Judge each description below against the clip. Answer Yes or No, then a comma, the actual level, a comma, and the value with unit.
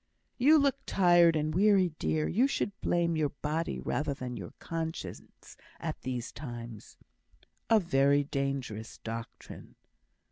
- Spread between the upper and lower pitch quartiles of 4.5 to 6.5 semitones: Yes, average, 5.1 semitones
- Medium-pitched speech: Yes, medium, 155 Hz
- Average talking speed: No, slow, 130 wpm